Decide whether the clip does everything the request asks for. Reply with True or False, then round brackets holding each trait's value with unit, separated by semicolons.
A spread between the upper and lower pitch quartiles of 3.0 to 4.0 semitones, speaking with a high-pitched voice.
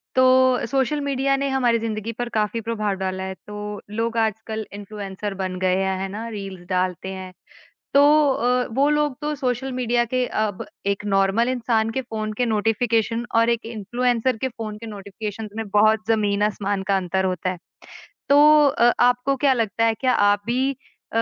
True (3.6 semitones; 225 Hz)